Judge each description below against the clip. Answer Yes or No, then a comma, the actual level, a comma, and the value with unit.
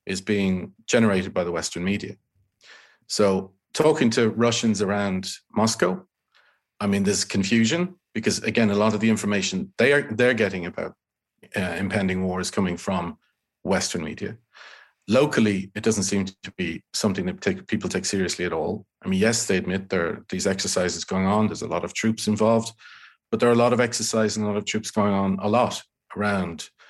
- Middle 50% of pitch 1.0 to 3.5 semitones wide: Yes, narrow, 2.4 semitones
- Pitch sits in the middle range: No, low, 105 Hz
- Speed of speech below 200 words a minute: Yes, average, 190 wpm